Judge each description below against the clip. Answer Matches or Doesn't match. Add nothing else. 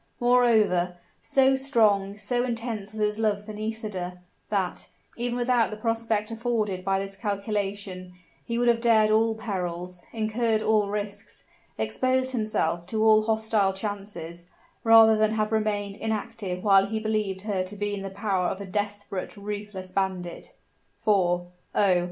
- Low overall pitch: Doesn't match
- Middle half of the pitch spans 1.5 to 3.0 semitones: Matches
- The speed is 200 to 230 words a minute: Doesn't match